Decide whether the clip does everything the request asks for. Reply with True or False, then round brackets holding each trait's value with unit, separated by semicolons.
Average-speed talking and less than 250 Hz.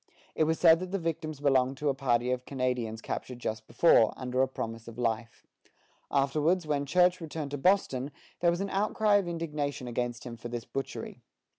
True (190 wpm; 140 Hz)